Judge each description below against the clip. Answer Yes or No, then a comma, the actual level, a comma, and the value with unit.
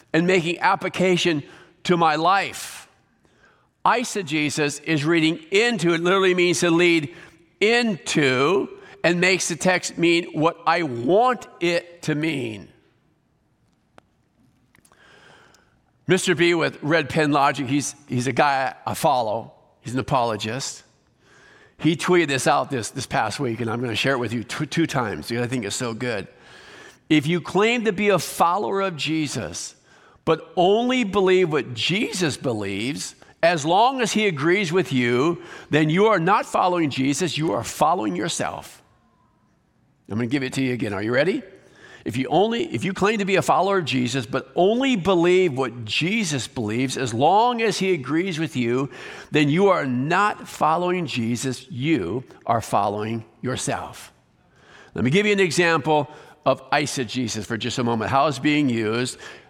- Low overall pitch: No, medium, 160 Hz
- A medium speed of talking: Yes, average, 165 wpm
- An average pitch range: No, wide, 5.8 semitones